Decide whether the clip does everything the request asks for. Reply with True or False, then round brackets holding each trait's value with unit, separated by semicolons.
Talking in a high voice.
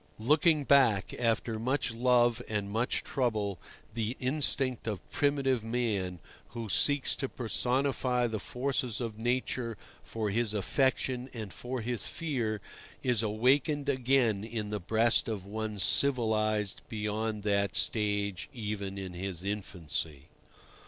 False (115 Hz)